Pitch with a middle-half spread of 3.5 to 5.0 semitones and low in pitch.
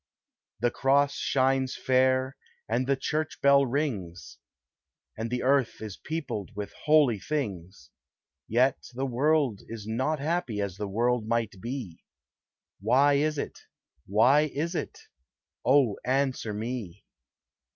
Yes: average, 4.3 semitones; low, 130 Hz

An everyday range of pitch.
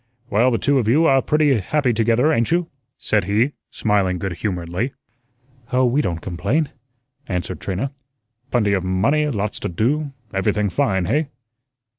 No: wide, 6.4 semitones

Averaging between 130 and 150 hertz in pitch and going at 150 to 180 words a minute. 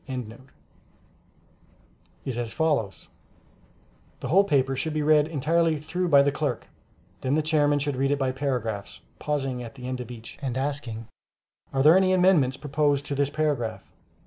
Yes: medium, 140 Hz; average, 165 wpm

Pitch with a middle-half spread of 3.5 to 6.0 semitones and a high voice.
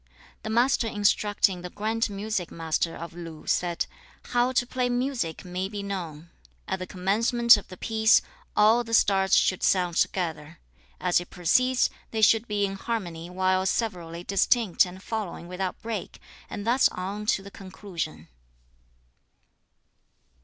Yes: average, 3.8 semitones; high, 195 Hz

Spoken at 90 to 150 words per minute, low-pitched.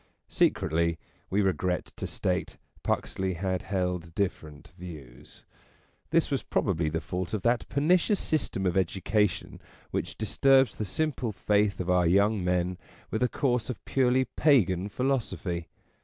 Yes: average, 140 wpm; very low, 95 Hz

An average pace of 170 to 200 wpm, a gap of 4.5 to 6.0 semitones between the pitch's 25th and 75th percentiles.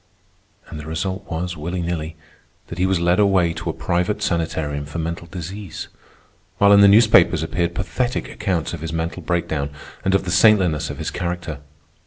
No: average, 180 wpm; average, 2.8 semitones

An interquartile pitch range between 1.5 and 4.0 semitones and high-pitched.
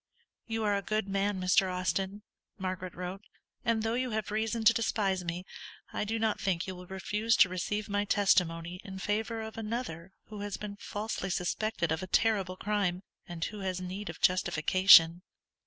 Yes: average, 2.8 semitones; high, 195 Hz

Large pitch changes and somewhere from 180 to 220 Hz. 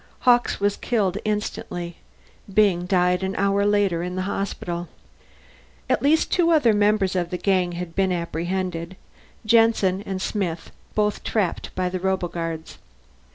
No: average, 2.7 semitones; high, 190 Hz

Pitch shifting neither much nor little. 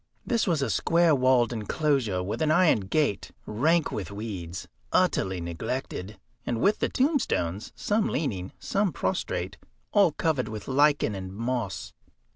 No: wide, 8.0 semitones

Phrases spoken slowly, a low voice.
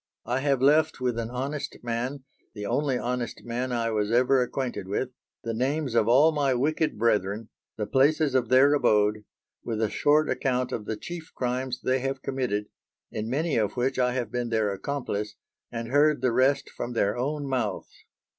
No: average, 185 wpm; low, 125 Hz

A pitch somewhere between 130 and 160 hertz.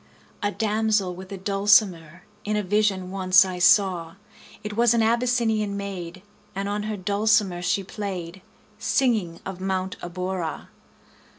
No: high, 195 Hz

